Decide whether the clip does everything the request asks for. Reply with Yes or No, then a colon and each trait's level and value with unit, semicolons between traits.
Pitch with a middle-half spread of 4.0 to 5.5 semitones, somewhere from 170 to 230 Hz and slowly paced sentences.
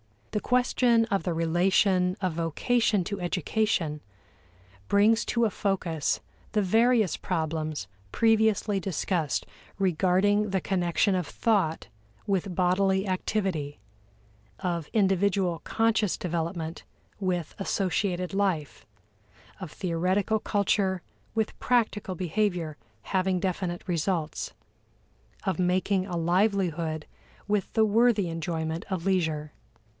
No: average, 3.3 semitones; medium, 185 Hz; slow, 105 wpm